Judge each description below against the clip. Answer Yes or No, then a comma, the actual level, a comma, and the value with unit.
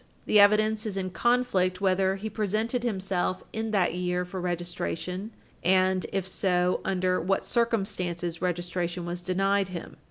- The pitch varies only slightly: Yes, narrow, 2.3 semitones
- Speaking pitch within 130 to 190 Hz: Yes, medium, 185 Hz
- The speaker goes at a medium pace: Yes, average, 145 wpm